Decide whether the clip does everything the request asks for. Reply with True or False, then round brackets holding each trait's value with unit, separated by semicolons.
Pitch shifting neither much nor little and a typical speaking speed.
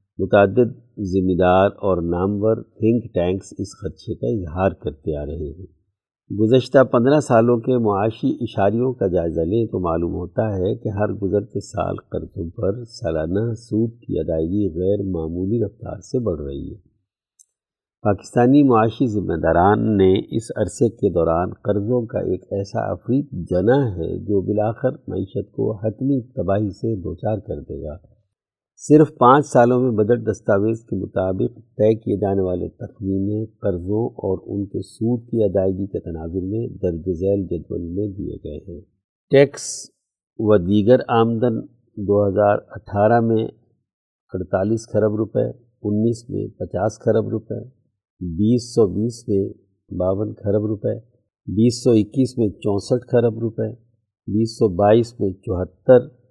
True (3.5 semitones; 145 wpm)